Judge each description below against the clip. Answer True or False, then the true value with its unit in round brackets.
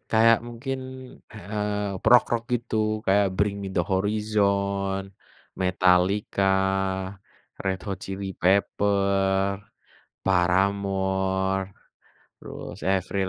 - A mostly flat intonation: True (1.4 semitones)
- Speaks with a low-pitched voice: True (100 Hz)